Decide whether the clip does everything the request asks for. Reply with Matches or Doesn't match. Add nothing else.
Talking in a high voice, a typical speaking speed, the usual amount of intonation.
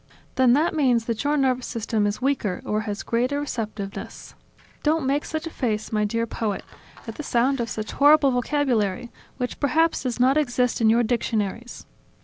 Matches